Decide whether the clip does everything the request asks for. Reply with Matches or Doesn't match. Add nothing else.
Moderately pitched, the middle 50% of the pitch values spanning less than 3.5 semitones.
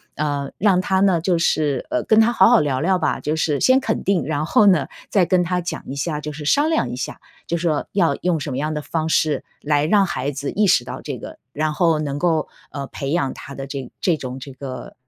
Doesn't match